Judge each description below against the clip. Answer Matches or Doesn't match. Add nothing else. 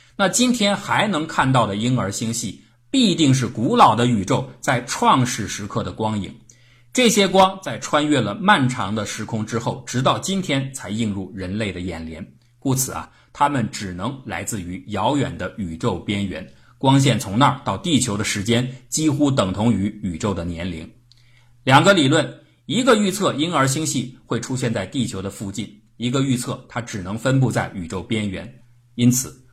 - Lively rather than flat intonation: Doesn't match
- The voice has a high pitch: Doesn't match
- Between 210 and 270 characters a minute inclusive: Matches